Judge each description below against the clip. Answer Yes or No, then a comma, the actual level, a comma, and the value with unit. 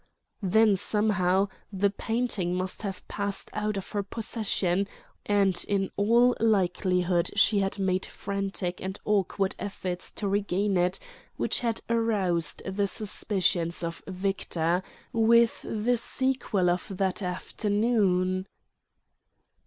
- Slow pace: Yes, slow, 115 wpm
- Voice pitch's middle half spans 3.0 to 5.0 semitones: No, narrow, 2.4 semitones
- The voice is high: Yes, high, 195 Hz